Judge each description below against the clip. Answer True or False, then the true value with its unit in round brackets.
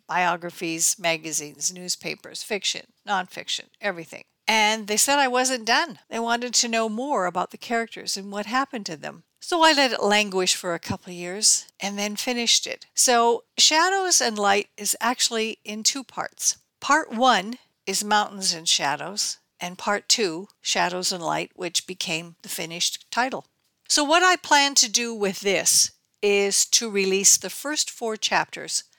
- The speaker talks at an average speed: True (165 wpm)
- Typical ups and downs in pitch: True (4.8 semitones)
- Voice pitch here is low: False (210 Hz)